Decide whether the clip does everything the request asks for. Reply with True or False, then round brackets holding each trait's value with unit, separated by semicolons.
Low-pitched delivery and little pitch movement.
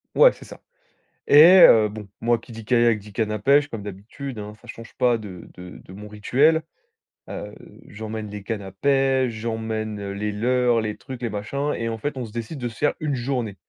False (115 Hz; 3.2 semitones)